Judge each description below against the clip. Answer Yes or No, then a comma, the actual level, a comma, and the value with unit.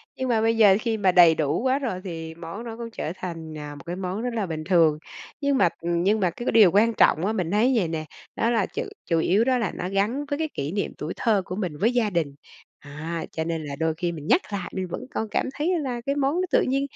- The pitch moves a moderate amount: No, wide, 6.0 semitones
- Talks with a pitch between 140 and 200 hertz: Yes, high, 190 Hz